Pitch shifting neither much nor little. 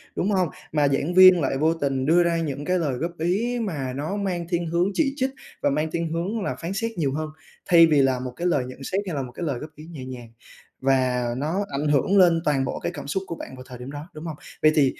Yes: average, 4.4 semitones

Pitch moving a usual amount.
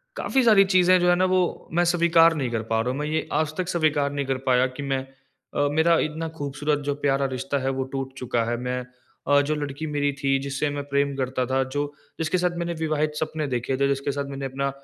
Yes: average, 3.0 semitones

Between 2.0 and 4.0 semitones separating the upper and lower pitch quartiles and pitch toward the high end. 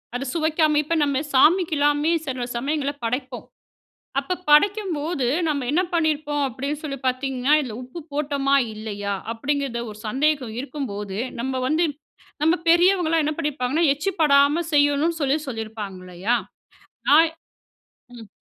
Yes: average, 3.4 semitones; very high, 285 Hz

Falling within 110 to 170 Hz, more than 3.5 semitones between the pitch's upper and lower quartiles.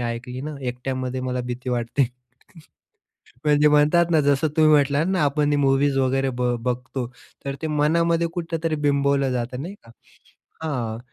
No: medium, 140 Hz; average, 3.2 semitones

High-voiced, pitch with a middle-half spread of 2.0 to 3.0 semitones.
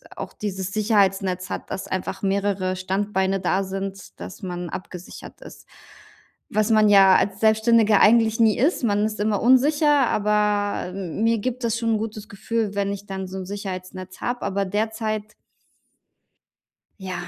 Yes: high, 205 Hz; narrow, 2.4 semitones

